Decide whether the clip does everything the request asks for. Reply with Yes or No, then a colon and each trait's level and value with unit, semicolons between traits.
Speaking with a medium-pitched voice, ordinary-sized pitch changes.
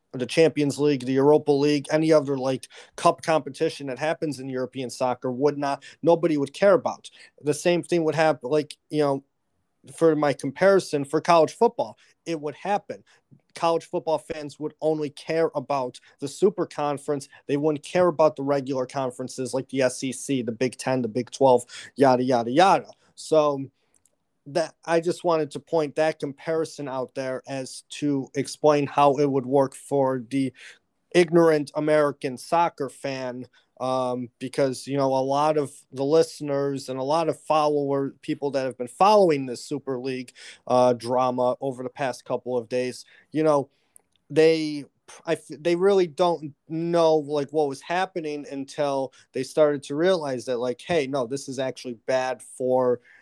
Yes: medium, 145 Hz; average, 3.1 semitones